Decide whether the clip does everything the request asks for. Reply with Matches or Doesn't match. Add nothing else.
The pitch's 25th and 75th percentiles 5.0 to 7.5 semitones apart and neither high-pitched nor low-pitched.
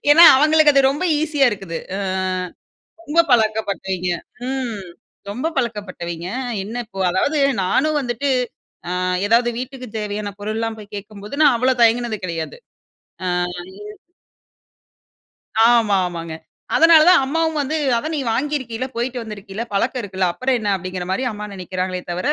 Doesn't match